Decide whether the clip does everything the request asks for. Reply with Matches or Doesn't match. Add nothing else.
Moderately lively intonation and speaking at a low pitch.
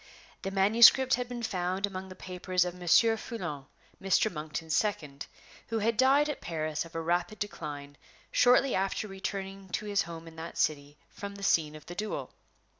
Doesn't match